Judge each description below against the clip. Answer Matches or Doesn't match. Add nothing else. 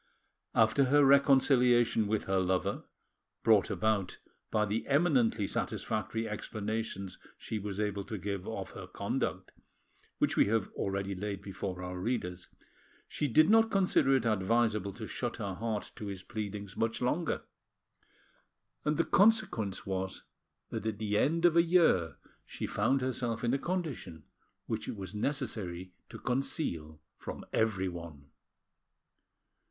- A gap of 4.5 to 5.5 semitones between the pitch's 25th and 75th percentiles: Matches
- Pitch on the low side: Matches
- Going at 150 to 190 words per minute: Doesn't match